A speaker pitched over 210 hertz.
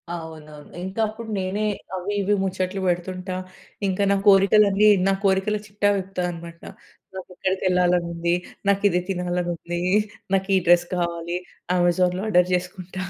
No: medium, 185 Hz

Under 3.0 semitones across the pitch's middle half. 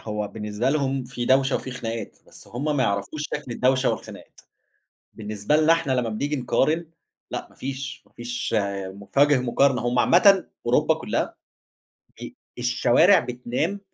No: average, 3.6 semitones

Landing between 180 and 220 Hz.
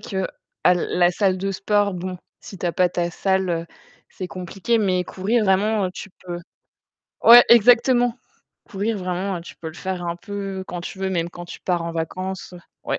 Yes: high, 190 Hz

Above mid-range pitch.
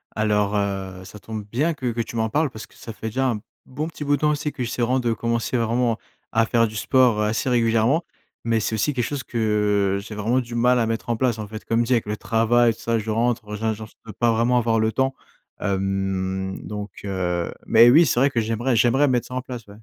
No: low, 115 Hz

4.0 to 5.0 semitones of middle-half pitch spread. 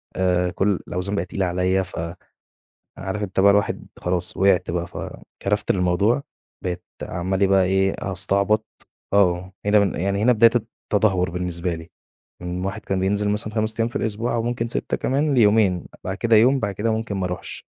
No: average, 2.9 semitones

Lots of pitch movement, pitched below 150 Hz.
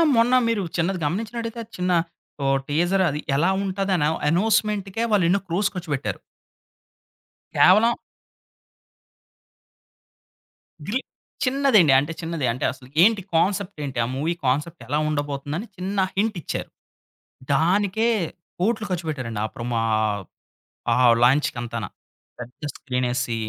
No: wide, 6.4 semitones; medium, 175 Hz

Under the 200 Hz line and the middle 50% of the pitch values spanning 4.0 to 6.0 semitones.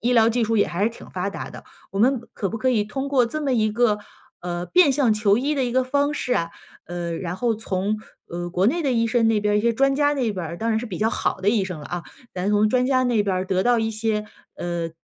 No: high, 220 Hz; average, 4.5 semitones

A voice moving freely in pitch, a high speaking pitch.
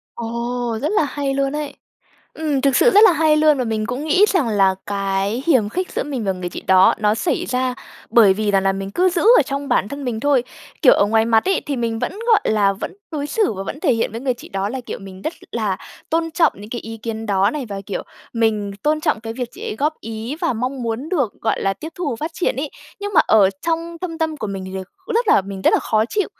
Yes: wide, 6.3 semitones; high, 240 Hz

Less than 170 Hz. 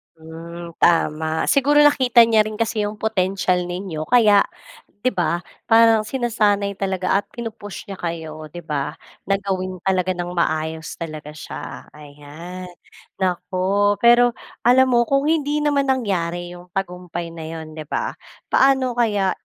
No: high, 190 Hz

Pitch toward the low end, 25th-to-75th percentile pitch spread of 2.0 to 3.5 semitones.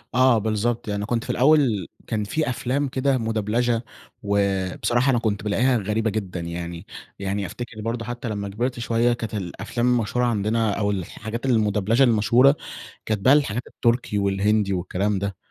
Yes: low, 110 Hz; average, 3.1 semitones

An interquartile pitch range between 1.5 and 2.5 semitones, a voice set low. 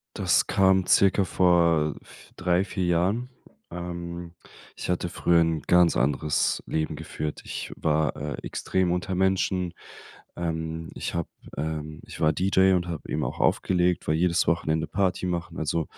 Yes: narrow, 2.2 semitones; very low, 85 Hz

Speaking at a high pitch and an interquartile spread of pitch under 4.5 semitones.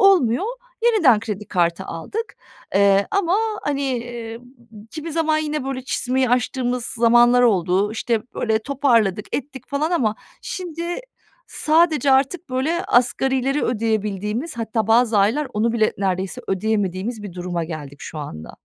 No: high, 240 Hz; average, 5.2 semitones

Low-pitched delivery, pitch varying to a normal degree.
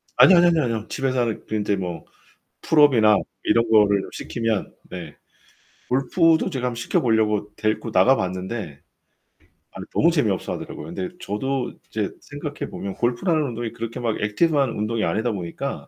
Yes: low, 115 Hz; average, 4.3 semitones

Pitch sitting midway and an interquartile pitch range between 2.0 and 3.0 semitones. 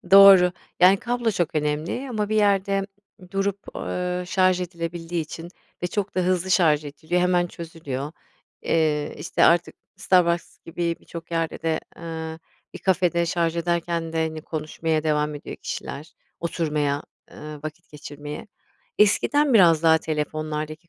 Yes: medium, 170 Hz; average, 2.7 semitones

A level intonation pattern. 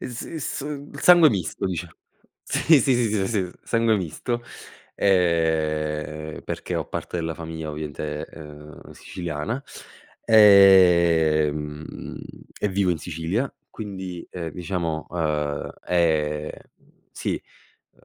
No: average, 4.5 semitones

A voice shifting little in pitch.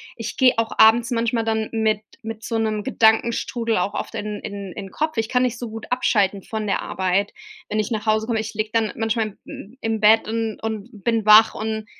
Yes: narrow, 1.2 semitones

